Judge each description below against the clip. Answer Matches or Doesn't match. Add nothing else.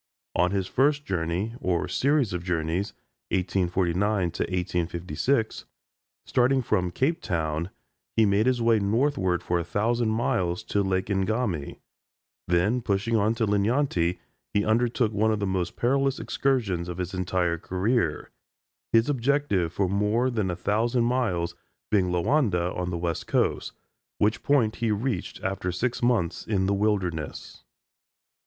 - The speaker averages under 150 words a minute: Matches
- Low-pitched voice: Matches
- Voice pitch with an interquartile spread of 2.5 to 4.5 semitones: Doesn't match